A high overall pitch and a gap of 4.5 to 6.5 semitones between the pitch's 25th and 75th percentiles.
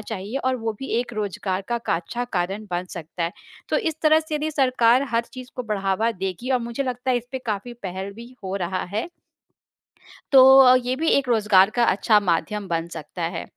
Yes: high, 225 Hz; average, 4.9 semitones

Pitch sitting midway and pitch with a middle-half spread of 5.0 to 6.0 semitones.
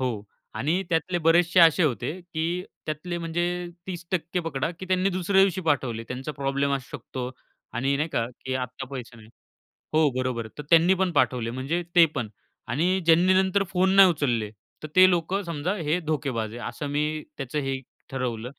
Yes: medium, 155 Hz; average, 5.3 semitones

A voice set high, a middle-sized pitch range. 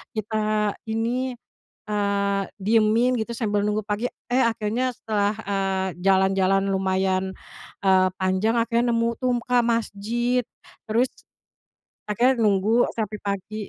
Yes: high, 215 Hz; average, 3.0 semitones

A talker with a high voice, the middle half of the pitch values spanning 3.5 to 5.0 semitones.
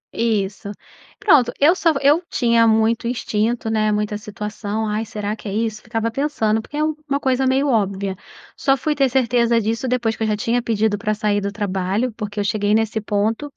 No: high, 225 Hz; average, 3.0 semitones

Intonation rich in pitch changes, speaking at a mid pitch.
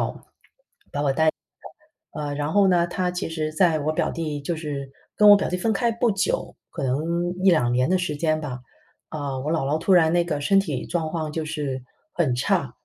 No: average, 3.6 semitones; medium, 160 Hz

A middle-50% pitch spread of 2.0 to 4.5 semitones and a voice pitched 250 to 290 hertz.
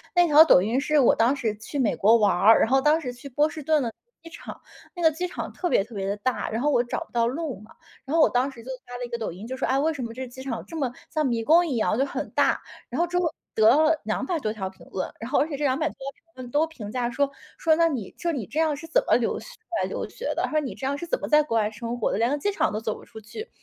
No: average, 5.2 semitones; very high, 265 Hz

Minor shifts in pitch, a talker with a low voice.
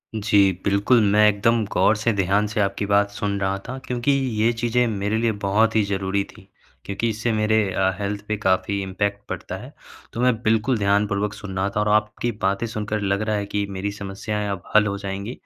Yes: narrow, 1.6 semitones; low, 105 Hz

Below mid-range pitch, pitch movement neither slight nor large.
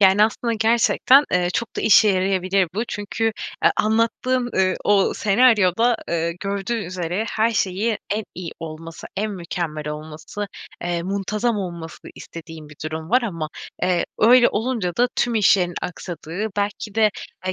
No: high, 195 Hz; average, 4.2 semitones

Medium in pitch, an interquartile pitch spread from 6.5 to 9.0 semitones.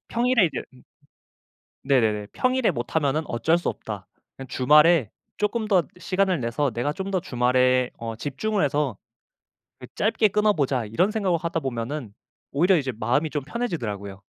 Yes: medium, 145 Hz; wide, 7.3 semitones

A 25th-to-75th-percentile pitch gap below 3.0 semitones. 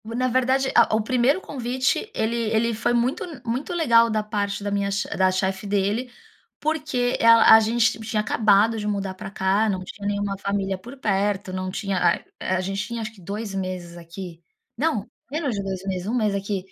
No: average, 3.4 semitones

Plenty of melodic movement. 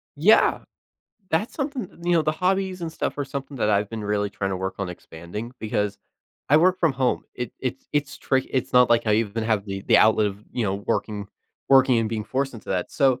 Yes: wide, 5.7 semitones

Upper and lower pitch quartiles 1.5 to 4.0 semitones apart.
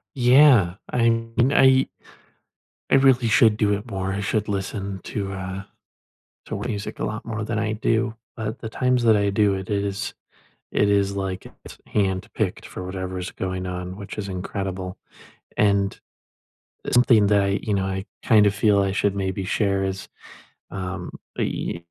Yes: narrow, 2.5 semitones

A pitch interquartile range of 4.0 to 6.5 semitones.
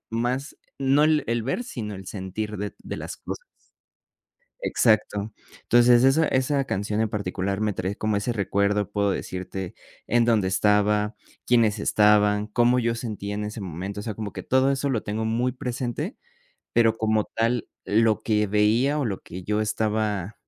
No: average, 2.8 semitones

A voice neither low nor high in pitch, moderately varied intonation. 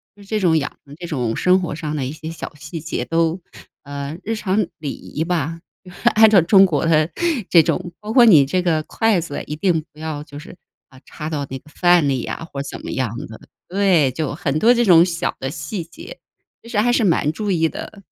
Yes: medium, 165 Hz; average, 3.9 semitones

